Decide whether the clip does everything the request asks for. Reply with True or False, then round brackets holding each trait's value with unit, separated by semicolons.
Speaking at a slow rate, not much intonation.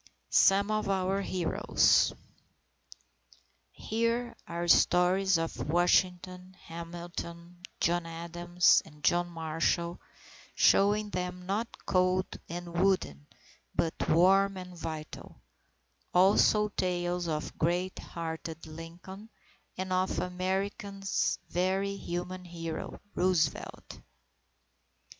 True (90 wpm; 2.0 semitones)